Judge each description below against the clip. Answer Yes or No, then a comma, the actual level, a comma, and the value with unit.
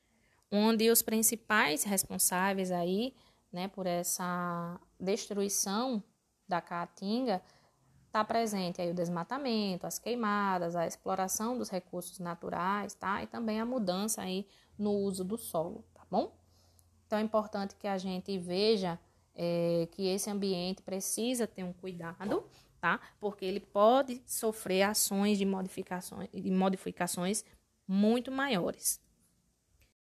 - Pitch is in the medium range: No, high, 195 Hz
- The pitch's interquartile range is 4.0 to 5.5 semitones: No, average, 3.3 semitones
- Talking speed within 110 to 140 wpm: Yes, average, 125 wpm